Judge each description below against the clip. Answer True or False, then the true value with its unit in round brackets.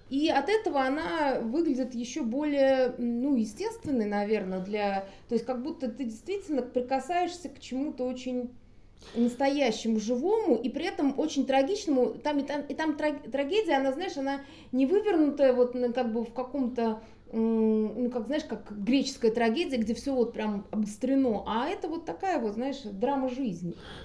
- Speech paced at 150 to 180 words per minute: True (160 wpm)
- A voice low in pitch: False (260 Hz)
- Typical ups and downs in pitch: True (3.5 semitones)